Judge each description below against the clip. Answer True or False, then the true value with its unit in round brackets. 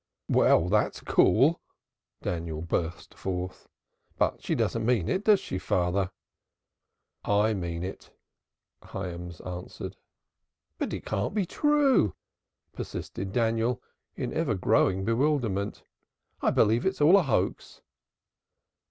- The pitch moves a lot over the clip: True (5.7 semitones)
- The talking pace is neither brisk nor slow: False (115 wpm)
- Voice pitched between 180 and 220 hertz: False (100 Hz)